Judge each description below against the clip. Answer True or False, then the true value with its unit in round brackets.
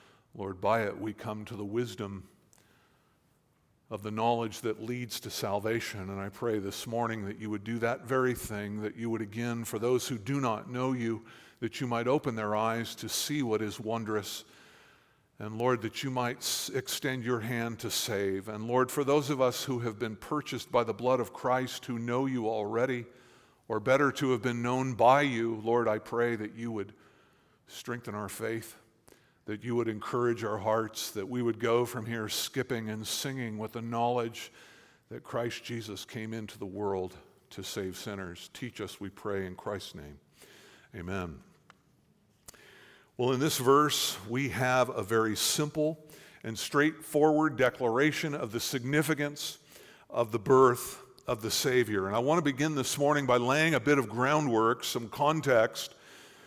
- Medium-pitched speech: False (115 Hz)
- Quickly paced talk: False (175 wpm)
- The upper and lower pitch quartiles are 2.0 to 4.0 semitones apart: True (2.9 semitones)